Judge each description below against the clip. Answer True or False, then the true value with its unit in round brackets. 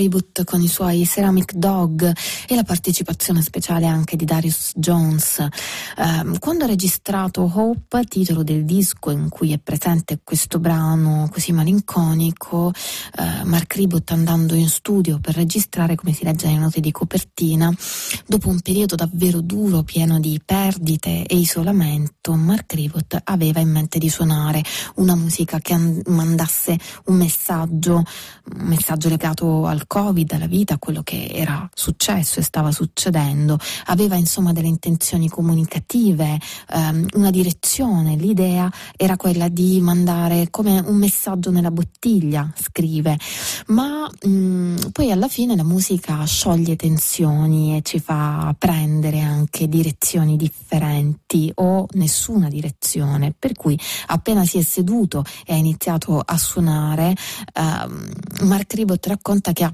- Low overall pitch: False (170 Hz)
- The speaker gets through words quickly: False (140 wpm)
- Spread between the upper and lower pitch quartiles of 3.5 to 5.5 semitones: False (2.6 semitones)